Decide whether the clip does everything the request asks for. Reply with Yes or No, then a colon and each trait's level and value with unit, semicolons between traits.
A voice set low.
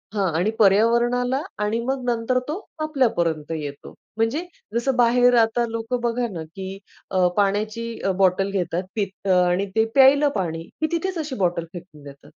No: high, 225 Hz